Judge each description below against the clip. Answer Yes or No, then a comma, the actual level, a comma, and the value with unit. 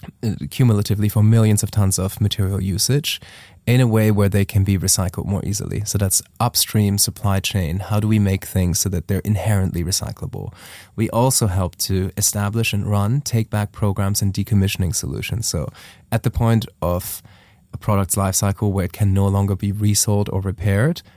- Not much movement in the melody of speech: Yes, narrow, 2.0 semitones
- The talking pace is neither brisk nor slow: Yes, average, 180 wpm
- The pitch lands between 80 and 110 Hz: Yes, low, 100 Hz